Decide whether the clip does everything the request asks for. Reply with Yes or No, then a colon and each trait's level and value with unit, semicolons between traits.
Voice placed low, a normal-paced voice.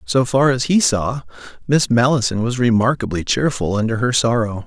Yes: low, 120 Hz; average, 165 wpm